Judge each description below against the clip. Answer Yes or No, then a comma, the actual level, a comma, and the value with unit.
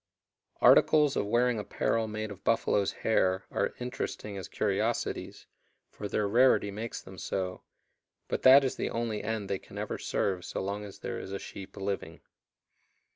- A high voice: No, low, 105 Hz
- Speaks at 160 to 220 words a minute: Yes, average, 165 wpm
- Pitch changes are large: No, average, 2.8 semitones